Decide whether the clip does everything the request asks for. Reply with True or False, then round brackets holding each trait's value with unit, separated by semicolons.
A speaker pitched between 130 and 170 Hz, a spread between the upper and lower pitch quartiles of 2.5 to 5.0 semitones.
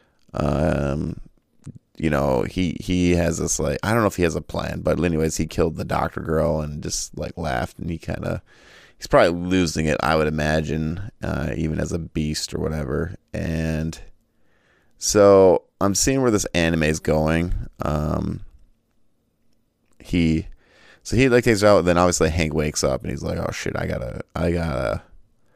False (80 Hz; 2.9 semitones)